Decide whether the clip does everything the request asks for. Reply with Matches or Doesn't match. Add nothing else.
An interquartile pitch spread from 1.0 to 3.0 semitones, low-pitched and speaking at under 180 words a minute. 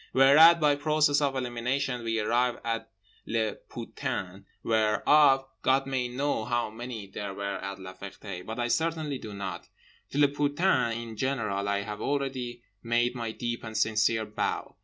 Doesn't match